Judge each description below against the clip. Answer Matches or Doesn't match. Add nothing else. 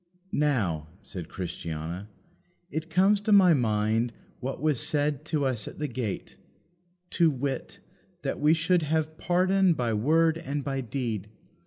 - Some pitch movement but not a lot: Doesn't match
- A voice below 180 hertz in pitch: Matches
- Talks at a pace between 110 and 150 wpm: Matches